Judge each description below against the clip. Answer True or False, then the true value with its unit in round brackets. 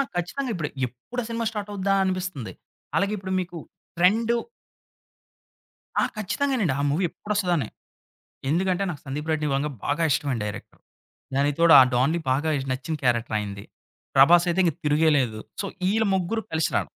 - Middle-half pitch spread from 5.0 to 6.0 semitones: True (5.5 semitones)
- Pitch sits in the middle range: True (170 Hz)